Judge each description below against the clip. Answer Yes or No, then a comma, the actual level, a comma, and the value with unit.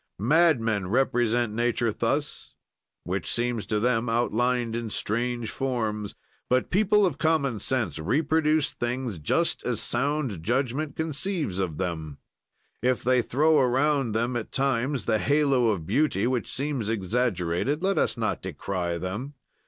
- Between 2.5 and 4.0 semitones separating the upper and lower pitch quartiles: No, average, 4.6 semitones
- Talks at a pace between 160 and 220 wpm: No, slow, 135 wpm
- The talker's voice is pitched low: Yes, low, 120 Hz